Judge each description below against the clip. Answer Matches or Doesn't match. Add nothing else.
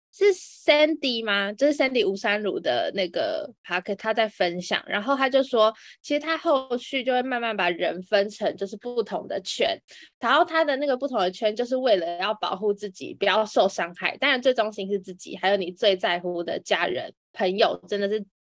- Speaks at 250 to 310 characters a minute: Doesn't match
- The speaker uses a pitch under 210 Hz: Doesn't match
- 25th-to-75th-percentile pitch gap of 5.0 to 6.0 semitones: Matches